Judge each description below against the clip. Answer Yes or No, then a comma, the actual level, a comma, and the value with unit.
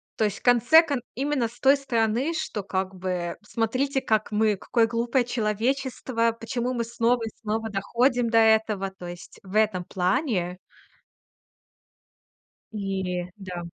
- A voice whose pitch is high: Yes, high, 225 Hz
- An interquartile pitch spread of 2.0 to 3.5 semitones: No, average, 3.9 semitones